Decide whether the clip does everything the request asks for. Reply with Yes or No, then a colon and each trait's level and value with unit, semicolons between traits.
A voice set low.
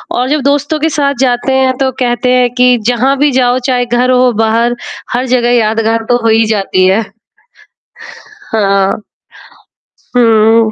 No: high, 245 Hz